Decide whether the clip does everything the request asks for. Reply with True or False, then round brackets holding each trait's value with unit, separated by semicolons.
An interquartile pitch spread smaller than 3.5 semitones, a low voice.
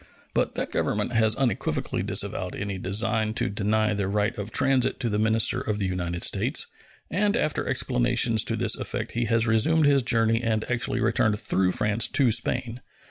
True (2.7 semitones; 110 Hz)